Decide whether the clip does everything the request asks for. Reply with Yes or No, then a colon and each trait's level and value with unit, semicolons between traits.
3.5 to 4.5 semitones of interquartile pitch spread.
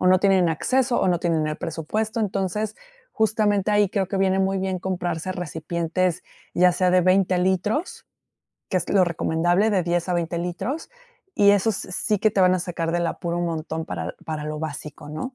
No: average, 2.9 semitones